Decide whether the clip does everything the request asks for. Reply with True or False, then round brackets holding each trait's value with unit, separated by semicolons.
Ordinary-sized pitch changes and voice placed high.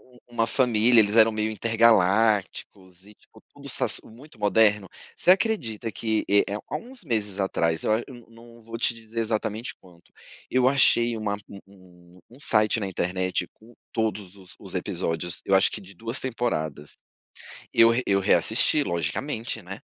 False (3.3 semitones; 110 Hz)